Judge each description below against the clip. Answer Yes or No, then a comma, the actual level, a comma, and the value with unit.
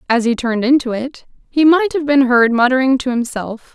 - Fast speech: Yes, fast, 210 wpm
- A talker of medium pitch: No, very high, 260 Hz